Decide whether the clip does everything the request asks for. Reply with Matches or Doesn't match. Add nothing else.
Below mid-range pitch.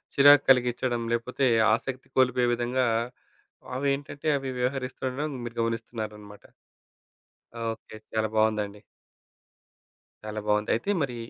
Matches